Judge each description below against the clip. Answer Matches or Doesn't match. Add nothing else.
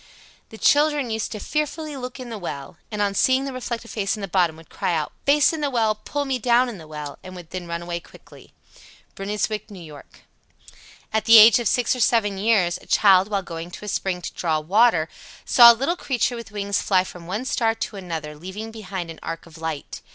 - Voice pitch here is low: Doesn't match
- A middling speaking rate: Doesn't match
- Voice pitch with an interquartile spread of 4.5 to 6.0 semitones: Matches